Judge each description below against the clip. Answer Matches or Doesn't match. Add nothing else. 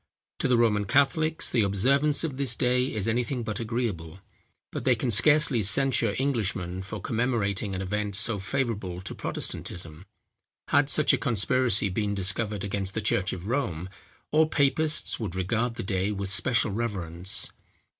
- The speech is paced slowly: Doesn't match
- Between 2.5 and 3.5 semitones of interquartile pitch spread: Doesn't match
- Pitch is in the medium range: Doesn't match